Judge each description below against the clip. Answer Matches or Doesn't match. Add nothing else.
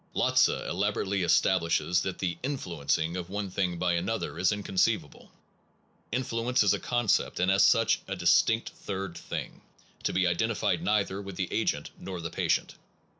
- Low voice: Matches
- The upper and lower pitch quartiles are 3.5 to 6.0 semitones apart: Doesn't match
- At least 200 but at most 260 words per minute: Doesn't match